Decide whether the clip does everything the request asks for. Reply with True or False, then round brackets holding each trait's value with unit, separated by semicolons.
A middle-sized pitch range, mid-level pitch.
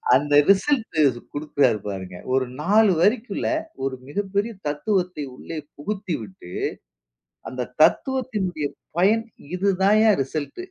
False (6.7 semitones; 180 Hz)